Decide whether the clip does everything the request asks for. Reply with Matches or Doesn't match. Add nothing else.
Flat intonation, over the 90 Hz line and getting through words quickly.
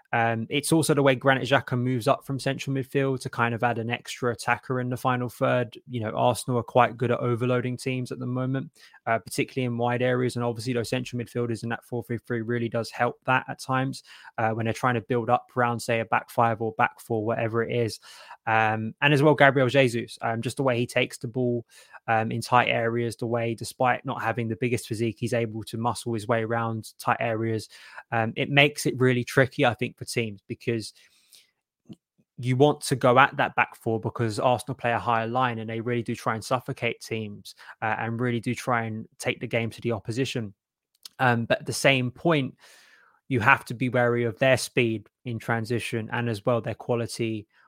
Matches